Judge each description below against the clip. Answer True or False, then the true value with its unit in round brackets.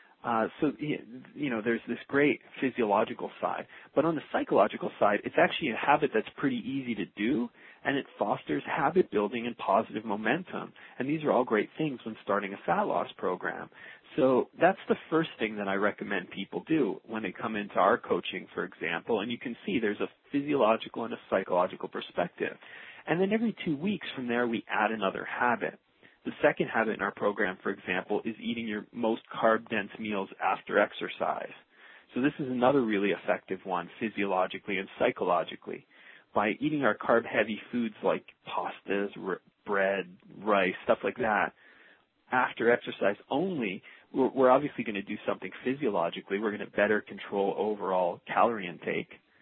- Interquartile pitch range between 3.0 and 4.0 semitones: False (5.2 semitones)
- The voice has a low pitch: True (110 Hz)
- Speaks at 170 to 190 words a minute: True (175 wpm)